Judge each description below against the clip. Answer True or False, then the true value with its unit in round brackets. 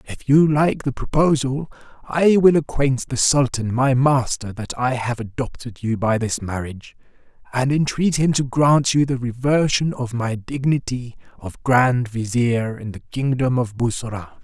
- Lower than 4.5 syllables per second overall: True (4.3 syllables/s)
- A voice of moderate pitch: False (130 Hz)